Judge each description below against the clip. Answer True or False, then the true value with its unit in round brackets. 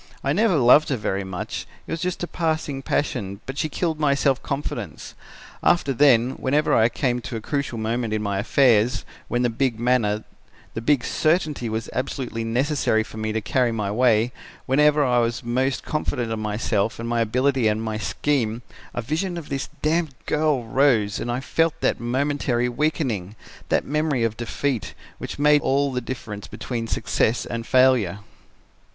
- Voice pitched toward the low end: True (125 Hz)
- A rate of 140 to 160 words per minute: False (175 wpm)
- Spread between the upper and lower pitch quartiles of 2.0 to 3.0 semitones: False (4.2 semitones)